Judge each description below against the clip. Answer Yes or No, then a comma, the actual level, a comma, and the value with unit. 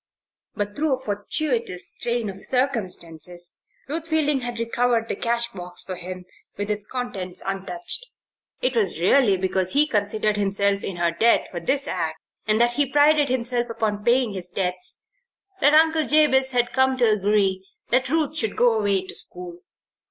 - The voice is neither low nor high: No, high, 220 Hz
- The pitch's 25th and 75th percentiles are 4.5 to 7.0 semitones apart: Yes, wide, 5.5 semitones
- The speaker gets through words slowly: No, average, 165 wpm